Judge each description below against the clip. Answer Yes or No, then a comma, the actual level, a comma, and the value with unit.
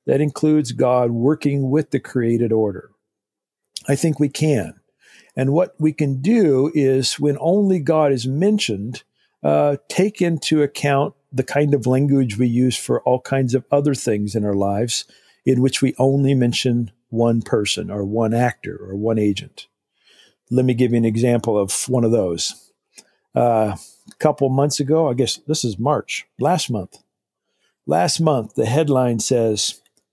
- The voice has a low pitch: Yes, low, 130 Hz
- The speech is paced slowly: No, average, 165 wpm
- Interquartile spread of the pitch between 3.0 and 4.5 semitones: Yes, average, 4.0 semitones